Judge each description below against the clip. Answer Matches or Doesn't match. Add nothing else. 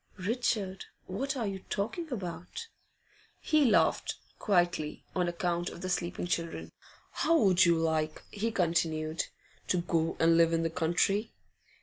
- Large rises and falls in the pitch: Doesn't match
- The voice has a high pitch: Doesn't match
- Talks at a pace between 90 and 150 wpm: Matches